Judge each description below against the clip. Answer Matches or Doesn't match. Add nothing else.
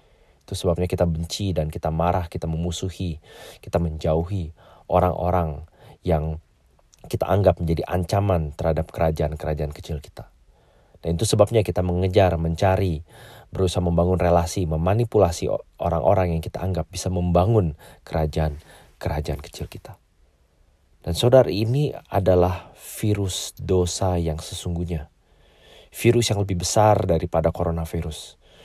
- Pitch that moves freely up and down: Doesn't match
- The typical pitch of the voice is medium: Doesn't match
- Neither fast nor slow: Doesn't match